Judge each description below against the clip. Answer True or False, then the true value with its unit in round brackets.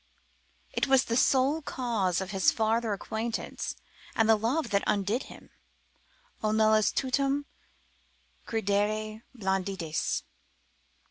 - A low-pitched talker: False (220 Hz)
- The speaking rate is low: True (110 wpm)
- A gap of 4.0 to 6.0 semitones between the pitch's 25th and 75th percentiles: False (3.4 semitones)